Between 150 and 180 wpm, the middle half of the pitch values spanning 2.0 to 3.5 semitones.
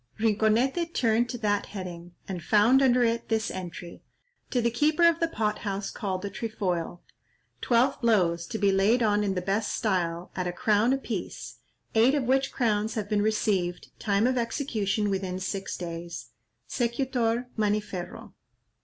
No: average, 160 wpm; average, 3.9 semitones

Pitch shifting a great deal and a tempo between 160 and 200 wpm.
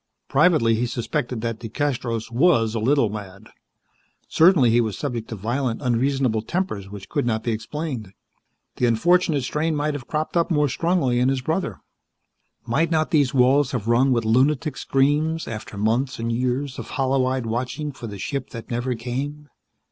No: average, 4.2 semitones; average, 170 wpm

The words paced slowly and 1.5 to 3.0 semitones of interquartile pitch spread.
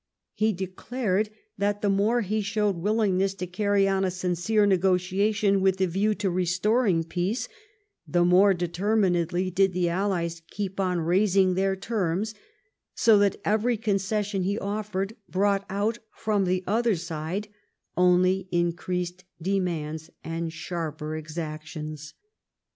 Yes: slow, 130 wpm; average, 2.7 semitones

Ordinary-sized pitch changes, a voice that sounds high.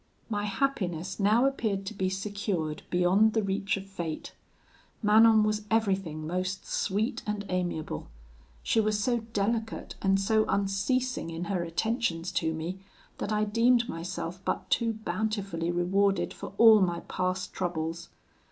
Yes: average, 3.5 semitones; high, 195 Hz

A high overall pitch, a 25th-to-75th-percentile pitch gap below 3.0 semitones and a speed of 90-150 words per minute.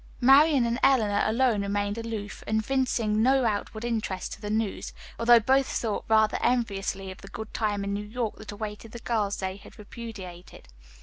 No: high, 220 Hz; narrow, 2.6 semitones; average, 175 wpm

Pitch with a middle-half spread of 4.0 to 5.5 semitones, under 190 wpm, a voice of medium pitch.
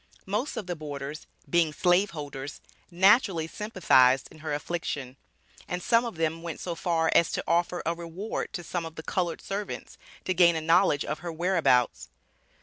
No: average, 2.7 semitones; average, 175 wpm; medium, 170 Hz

